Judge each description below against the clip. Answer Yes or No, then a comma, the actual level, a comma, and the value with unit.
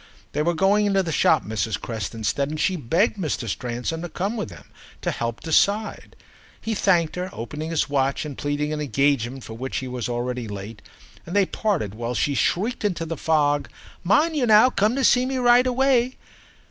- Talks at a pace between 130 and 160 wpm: No, average, 200 wpm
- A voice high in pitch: No, medium, 155 Hz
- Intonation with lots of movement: Yes, wide, 8.5 semitones